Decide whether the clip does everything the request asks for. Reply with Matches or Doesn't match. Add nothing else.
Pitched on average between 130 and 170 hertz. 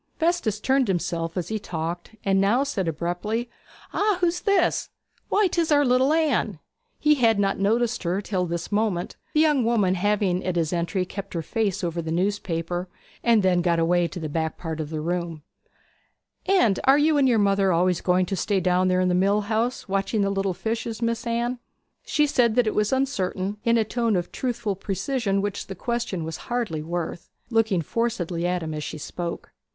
Doesn't match